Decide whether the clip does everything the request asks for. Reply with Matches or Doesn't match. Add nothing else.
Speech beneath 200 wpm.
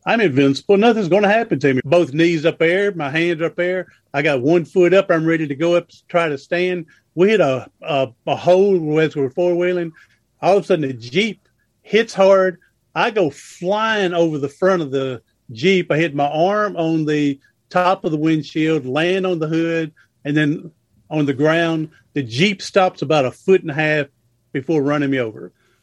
Doesn't match